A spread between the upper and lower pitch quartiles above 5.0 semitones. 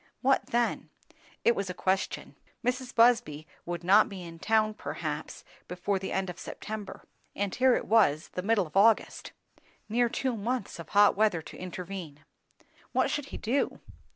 No: average, 4.3 semitones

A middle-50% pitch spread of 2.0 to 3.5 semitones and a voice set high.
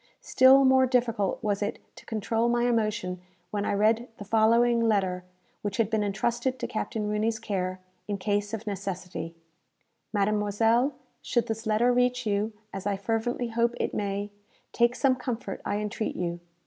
Yes: average, 2.7 semitones; high, 220 Hz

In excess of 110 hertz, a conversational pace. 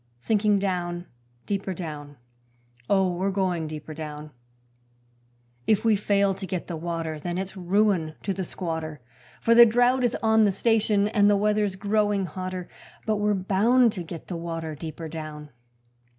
Yes: high, 190 Hz; average, 160 wpm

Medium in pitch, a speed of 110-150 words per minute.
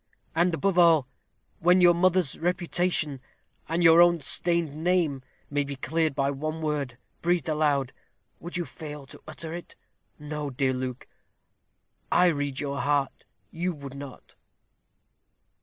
Yes: medium, 155 Hz; average, 140 wpm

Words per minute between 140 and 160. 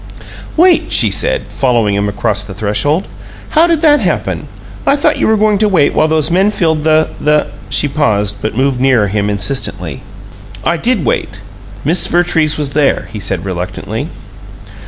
No: average, 175 wpm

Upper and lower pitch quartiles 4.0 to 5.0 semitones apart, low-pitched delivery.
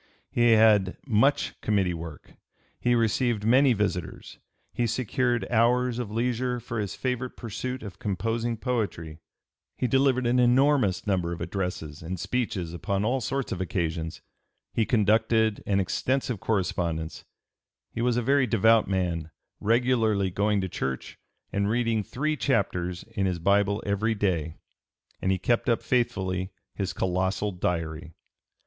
Yes: average, 4.6 semitones; low, 105 Hz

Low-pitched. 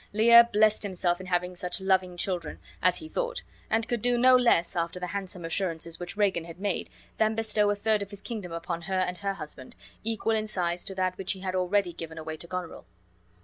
No: medium, 185 Hz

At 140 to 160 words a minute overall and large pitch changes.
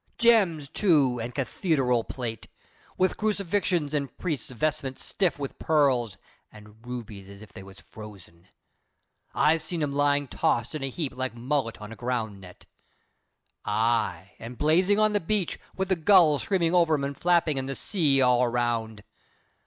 No: average, 170 wpm; wide, 6.0 semitones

